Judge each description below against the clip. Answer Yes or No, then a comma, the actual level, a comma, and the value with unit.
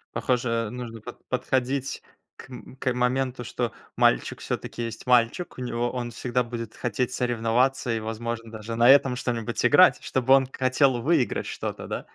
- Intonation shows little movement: Yes, narrow, 1.8 semitones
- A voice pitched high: No, low, 125 Hz